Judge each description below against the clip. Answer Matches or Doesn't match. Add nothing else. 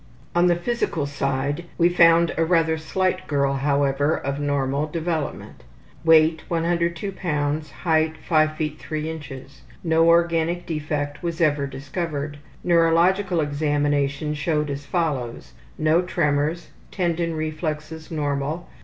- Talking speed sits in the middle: Doesn't match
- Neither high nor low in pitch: Matches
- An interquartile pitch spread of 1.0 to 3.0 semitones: Matches